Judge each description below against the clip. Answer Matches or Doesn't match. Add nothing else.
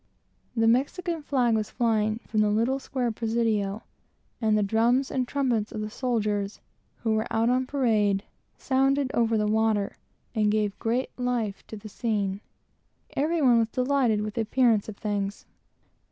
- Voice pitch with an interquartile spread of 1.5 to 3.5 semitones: Matches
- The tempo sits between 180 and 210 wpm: Doesn't match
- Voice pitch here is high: Matches